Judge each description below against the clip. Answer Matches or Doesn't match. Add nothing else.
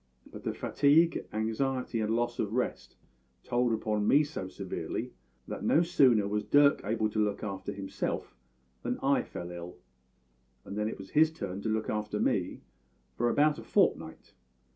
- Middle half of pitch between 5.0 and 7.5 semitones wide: Doesn't match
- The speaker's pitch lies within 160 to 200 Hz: Doesn't match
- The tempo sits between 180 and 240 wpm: Doesn't match